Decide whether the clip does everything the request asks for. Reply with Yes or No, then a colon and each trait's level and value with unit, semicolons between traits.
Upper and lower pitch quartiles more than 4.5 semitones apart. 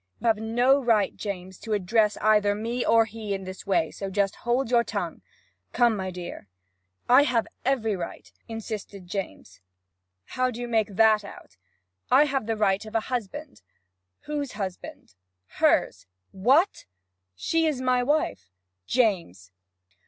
No: average, 4.0 semitones